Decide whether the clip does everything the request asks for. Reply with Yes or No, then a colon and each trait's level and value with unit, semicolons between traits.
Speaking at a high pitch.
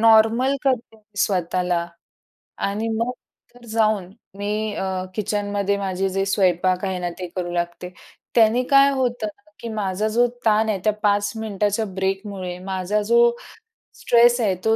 Yes: high, 205 Hz